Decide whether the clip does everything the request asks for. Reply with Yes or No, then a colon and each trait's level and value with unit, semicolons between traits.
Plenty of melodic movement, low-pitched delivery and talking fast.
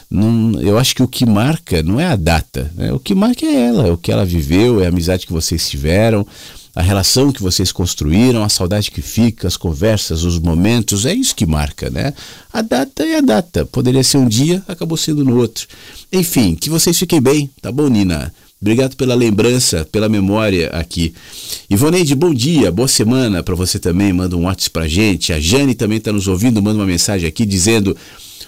Yes: wide, 6.2 semitones; low, 105 Hz; fast, 205 wpm